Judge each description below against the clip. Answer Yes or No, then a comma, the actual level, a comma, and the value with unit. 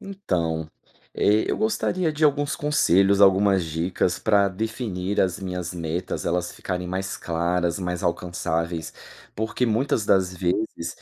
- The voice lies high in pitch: No, very low, 95 Hz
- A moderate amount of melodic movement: Yes, average, 3.8 semitones